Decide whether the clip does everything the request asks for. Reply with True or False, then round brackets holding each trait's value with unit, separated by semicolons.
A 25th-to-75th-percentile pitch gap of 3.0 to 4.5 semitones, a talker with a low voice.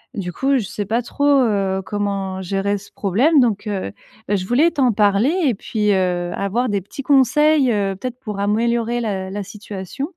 False (4.2 semitones; 210 Hz)